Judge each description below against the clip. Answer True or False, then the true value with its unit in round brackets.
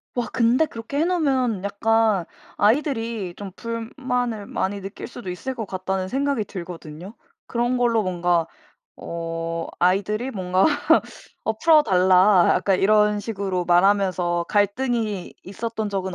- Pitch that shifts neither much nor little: True (4.1 semitones)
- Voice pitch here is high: True (205 Hz)